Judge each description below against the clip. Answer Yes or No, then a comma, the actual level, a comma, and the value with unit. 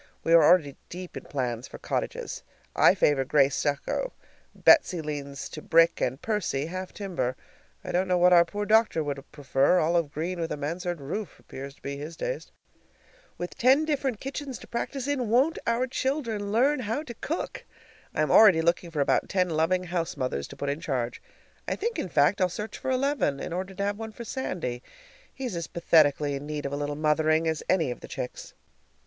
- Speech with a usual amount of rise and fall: No, wide, 7.0 semitones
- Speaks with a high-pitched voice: No, medium, 170 Hz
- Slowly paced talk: No, average, 200 wpm